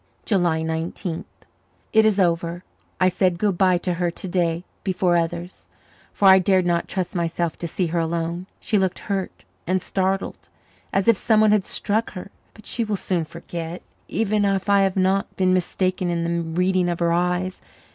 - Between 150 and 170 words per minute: No, average, 180 wpm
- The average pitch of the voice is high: No, medium, 180 Hz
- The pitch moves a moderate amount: No, narrow, 2.1 semitones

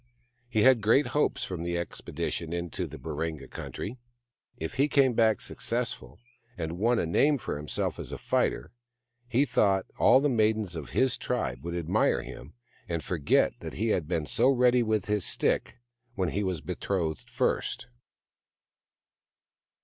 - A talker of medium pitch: No, low, 100 Hz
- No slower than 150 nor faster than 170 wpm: Yes, average, 160 wpm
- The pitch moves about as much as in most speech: No, wide, 6.4 semitones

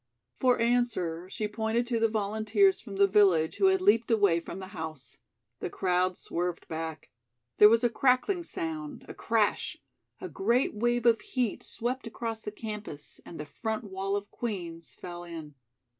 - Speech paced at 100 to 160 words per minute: No, average, 170 wpm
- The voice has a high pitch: Yes, high, 210 Hz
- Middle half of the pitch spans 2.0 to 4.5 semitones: No, average, 5.0 semitones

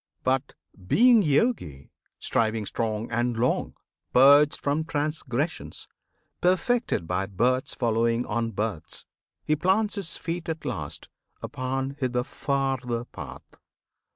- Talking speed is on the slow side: Yes, slow, 110 wpm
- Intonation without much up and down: No, average, 5.1 semitones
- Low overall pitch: Yes, low, 130 Hz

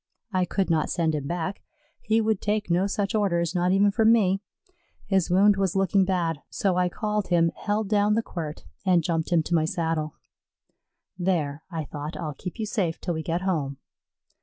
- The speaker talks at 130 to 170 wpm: No, average, 190 wpm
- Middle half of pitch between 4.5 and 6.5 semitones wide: No, average, 3.4 semitones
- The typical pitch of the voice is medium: Yes, medium, 180 Hz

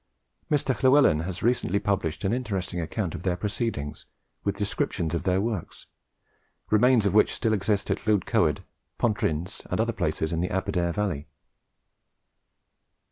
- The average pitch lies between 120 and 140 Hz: No, low, 100 Hz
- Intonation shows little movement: No, average, 4.1 semitones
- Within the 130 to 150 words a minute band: Yes, average, 140 wpm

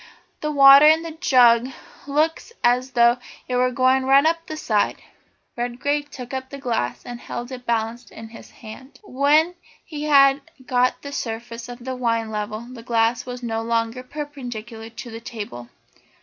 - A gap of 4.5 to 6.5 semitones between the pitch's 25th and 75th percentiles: No, average, 3.2 semitones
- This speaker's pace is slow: No, average, 175 wpm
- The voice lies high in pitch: Yes, very high, 250 Hz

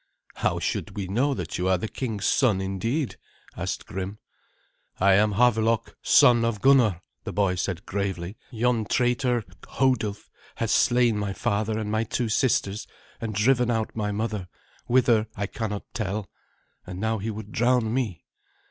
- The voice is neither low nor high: No, low, 110 Hz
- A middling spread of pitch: Yes, average, 3.1 semitones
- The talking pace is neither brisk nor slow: Yes, average, 155 wpm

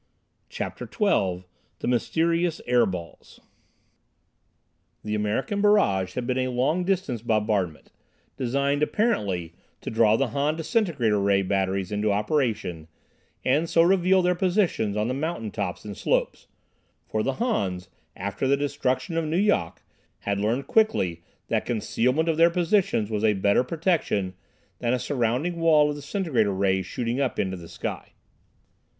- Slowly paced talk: No, average, 145 wpm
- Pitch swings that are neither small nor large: No, wide, 8.3 semitones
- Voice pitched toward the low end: Yes, low, 125 Hz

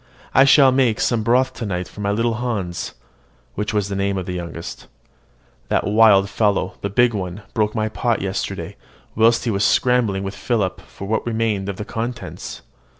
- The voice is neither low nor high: No, low, 105 Hz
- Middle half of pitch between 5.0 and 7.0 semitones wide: No, average, 3.1 semitones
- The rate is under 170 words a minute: No, average, 185 wpm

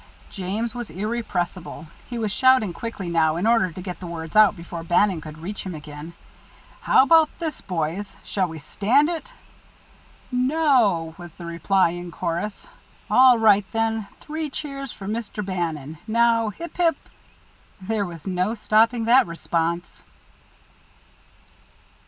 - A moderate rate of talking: Yes, average, 145 wpm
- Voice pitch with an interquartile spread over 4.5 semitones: Yes, wide, 5.5 semitones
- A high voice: Yes, high, 200 Hz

